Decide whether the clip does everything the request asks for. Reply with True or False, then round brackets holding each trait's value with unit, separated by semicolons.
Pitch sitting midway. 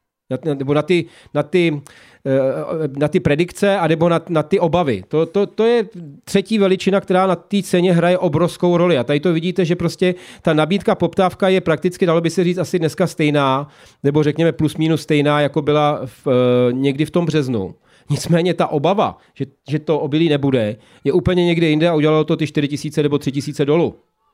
True (160 Hz)